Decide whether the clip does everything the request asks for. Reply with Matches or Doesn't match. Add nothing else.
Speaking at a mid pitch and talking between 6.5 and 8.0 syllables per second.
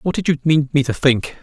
Doesn't match